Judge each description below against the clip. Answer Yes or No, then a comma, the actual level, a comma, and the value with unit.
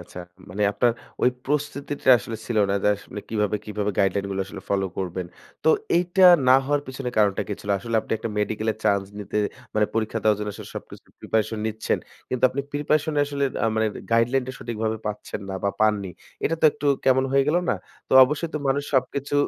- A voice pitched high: No, low, 110 Hz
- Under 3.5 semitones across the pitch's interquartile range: No, average, 4.8 semitones